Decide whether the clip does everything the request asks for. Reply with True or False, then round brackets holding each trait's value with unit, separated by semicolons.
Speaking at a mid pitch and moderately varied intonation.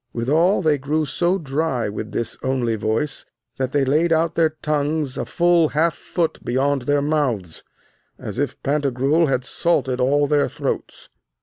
True (145 Hz; 3.3 semitones)